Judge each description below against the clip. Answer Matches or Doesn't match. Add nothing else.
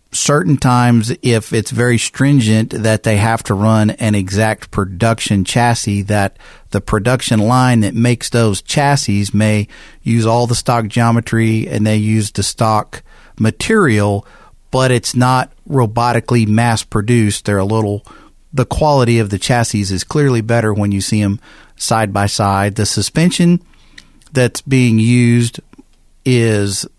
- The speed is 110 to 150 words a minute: Matches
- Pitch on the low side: Matches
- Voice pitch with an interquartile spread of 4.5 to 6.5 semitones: Doesn't match